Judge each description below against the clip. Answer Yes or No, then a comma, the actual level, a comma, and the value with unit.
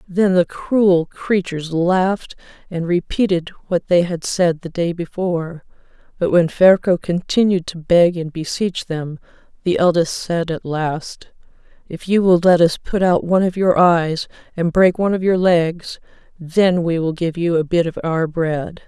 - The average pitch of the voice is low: No, medium, 175 Hz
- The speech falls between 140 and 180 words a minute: Yes, average, 175 wpm